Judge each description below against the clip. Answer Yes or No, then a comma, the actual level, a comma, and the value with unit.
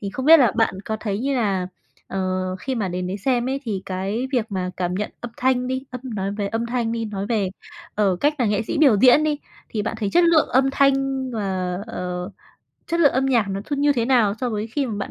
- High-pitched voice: Yes, high, 230 Hz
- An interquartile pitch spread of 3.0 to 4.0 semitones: No, average, 4.9 semitones